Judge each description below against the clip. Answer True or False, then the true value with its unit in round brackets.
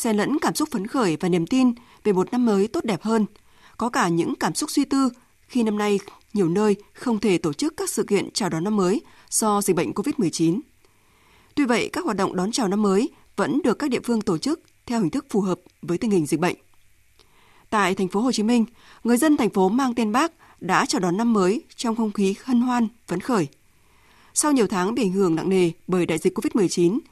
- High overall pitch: True (215 Hz)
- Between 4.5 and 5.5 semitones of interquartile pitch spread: True (5.2 semitones)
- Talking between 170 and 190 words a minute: False (235 wpm)